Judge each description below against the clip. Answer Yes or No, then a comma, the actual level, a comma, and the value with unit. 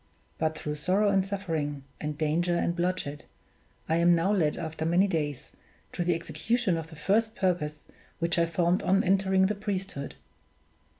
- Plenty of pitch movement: No, average, 3.4 semitones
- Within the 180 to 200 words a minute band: No, average, 165 wpm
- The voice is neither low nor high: Yes, medium, 175 Hz